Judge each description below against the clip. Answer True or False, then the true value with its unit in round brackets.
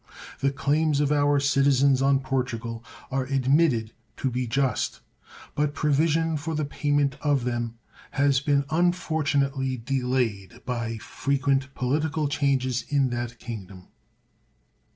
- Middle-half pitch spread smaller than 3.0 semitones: True (2.5 semitones)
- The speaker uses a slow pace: True (120 wpm)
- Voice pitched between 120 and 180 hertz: True (135 Hz)